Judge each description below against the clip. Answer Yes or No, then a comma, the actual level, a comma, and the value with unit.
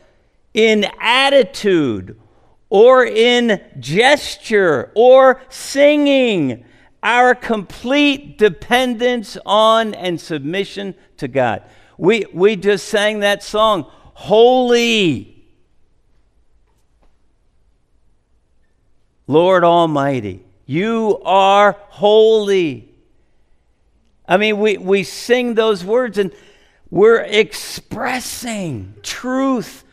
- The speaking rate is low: Yes, slow, 75 wpm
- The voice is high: Yes, high, 210 Hz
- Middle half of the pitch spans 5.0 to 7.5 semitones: Yes, average, 5.3 semitones